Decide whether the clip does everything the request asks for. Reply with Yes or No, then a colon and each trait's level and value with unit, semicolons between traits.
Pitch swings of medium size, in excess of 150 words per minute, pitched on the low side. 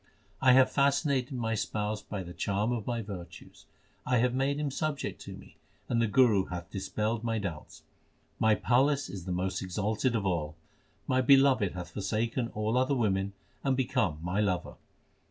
Yes: average, 4.9 semitones; average, 175 wpm; low, 110 Hz